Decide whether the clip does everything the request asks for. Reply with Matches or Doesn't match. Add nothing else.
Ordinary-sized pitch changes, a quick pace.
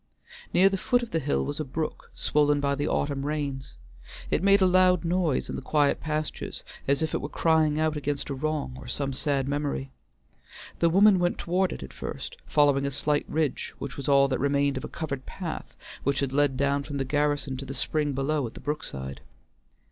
Doesn't match